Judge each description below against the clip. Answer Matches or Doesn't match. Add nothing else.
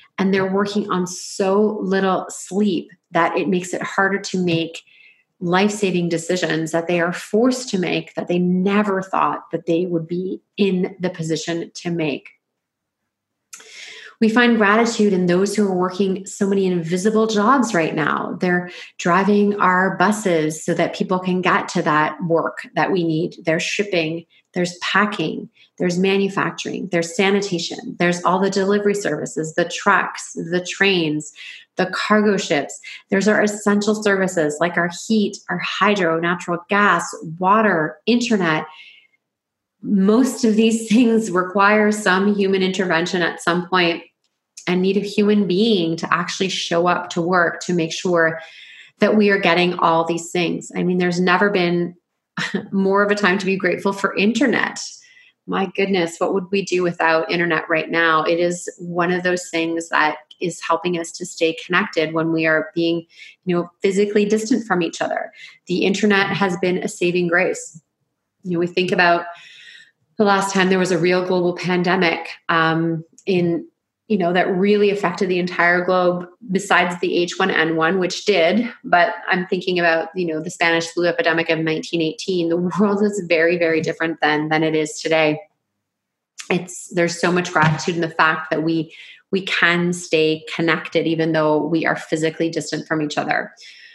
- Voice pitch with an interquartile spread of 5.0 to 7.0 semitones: Doesn't match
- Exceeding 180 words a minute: Doesn't match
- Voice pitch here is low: Doesn't match